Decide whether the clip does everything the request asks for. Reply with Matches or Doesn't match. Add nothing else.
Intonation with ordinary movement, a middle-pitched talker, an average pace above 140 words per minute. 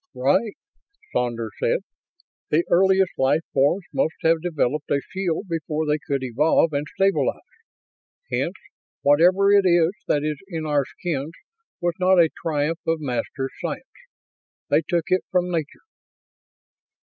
Doesn't match